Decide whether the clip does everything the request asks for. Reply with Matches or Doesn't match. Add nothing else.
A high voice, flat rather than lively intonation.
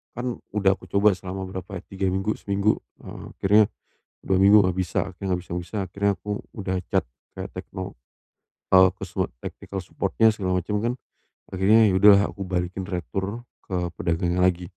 Doesn't match